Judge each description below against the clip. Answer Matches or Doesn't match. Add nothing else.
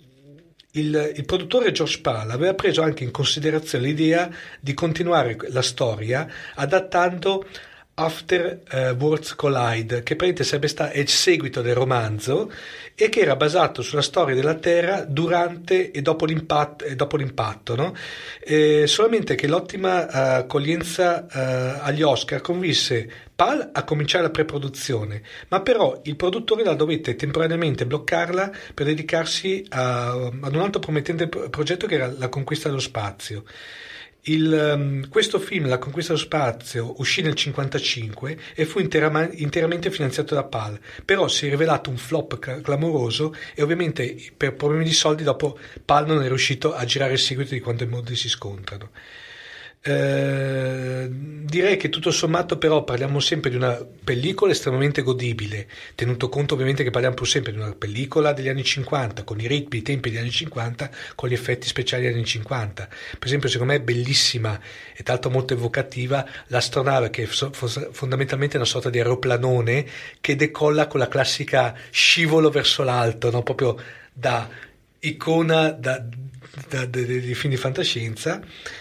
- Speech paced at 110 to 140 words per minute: Doesn't match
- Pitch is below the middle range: Doesn't match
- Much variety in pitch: Doesn't match